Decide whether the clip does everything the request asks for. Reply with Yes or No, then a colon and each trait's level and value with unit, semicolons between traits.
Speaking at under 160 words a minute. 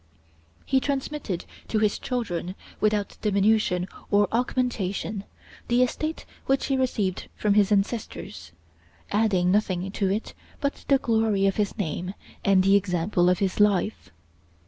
Yes: slow, 135 wpm